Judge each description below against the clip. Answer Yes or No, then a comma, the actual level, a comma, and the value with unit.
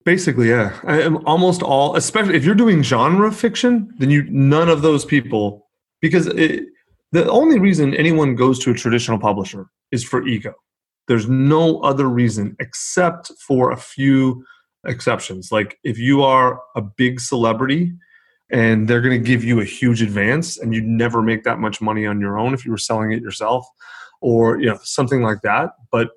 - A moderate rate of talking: Yes, average, 185 wpm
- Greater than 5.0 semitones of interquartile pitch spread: Yes, wide, 5.6 semitones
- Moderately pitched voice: No, low, 130 Hz